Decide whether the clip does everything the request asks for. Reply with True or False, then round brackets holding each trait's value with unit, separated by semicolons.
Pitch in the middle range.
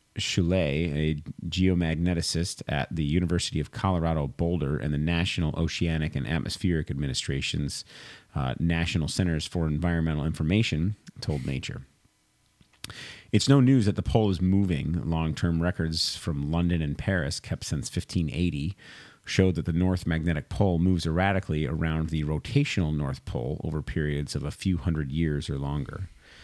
False (85 Hz)